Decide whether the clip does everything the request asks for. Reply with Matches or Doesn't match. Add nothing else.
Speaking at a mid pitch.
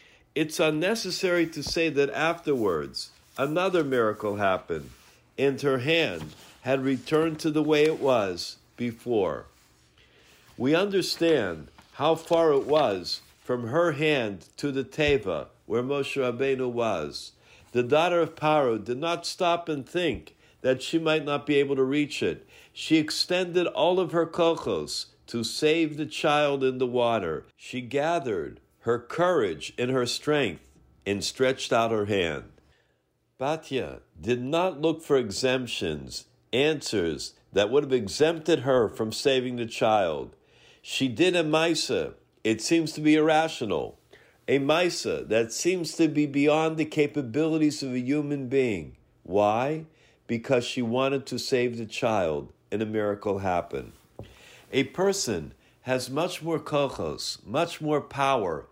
Matches